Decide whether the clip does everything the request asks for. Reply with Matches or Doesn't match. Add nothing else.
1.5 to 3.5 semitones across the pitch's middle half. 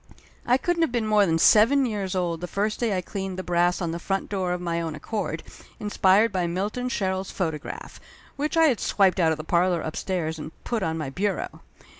Doesn't match